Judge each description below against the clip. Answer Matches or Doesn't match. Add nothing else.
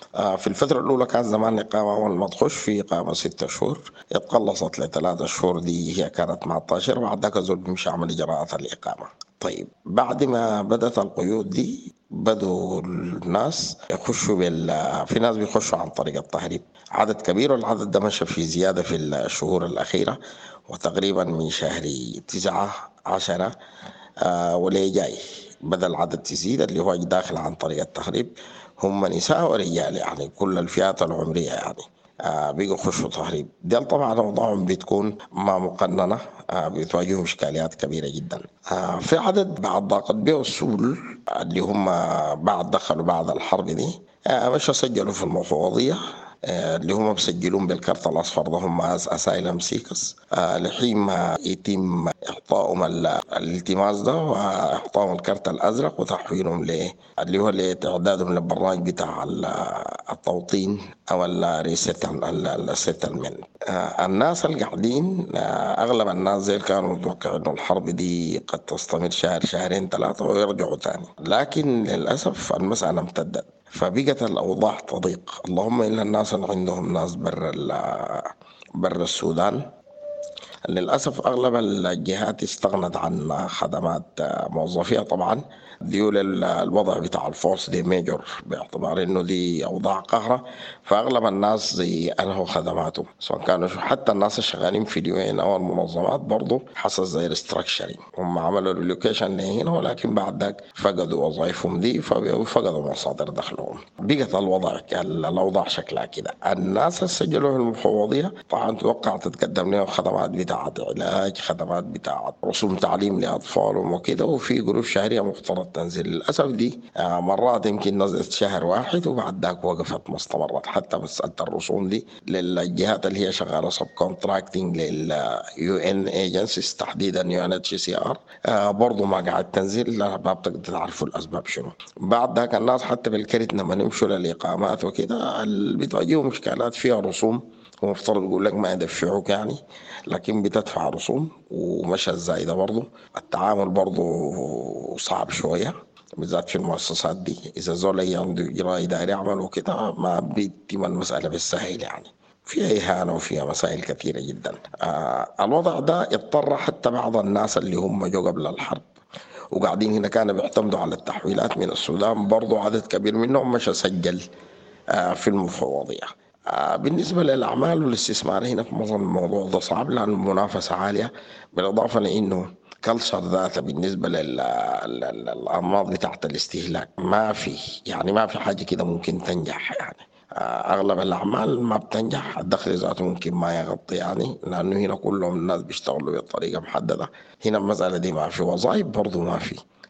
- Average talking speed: Doesn't match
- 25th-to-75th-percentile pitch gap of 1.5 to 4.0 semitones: Matches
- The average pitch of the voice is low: Matches